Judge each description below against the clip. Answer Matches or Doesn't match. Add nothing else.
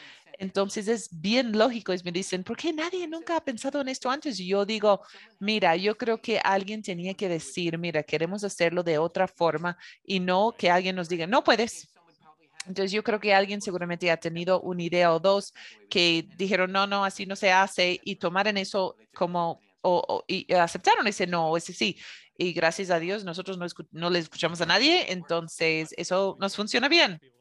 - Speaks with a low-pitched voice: Doesn't match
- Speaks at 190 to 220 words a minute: Matches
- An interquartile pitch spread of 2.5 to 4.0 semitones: Matches